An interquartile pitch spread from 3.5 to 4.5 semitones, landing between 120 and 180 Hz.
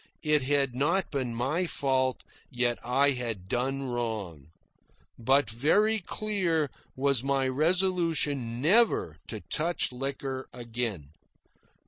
Yes: average, 4.1 semitones; low, 135 Hz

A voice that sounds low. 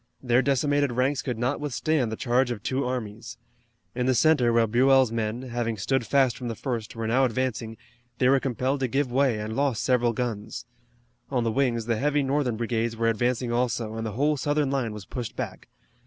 Yes: low, 125 Hz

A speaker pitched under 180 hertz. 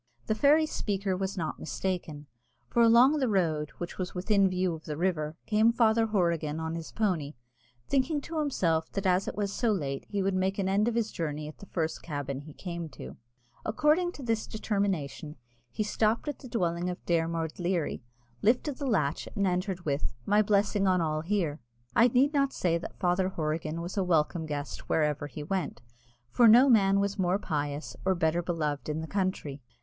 No: medium, 185 Hz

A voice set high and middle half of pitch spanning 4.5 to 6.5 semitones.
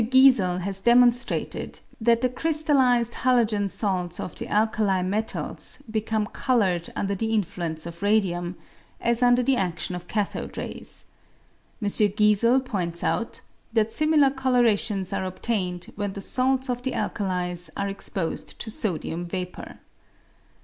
Yes: high, 210 Hz; average, 4.8 semitones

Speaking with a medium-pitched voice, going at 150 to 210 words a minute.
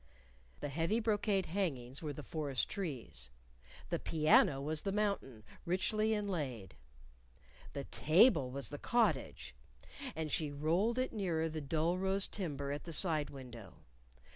No: medium, 160 Hz; average, 140 wpm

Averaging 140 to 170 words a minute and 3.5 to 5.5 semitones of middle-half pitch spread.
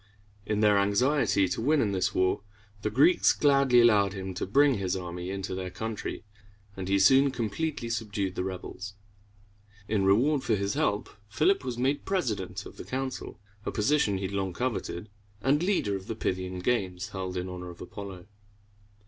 No: average, 180 wpm; average, 5.2 semitones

